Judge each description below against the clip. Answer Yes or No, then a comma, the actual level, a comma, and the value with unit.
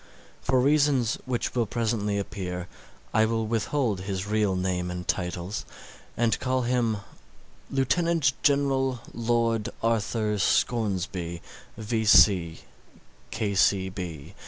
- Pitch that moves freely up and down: No, average, 4.4 semitones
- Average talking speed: No, slow, 95 wpm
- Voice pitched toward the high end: No, low, 110 Hz